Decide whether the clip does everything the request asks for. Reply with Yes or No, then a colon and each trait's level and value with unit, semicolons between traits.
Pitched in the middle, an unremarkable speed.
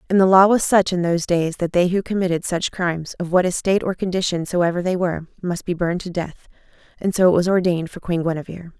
No: medium, 180 Hz; fast, 240 wpm